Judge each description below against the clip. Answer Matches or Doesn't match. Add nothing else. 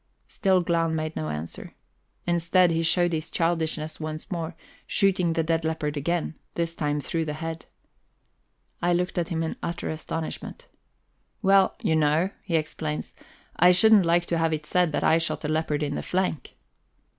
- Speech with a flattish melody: Matches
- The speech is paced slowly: Doesn't match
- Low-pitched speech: Doesn't match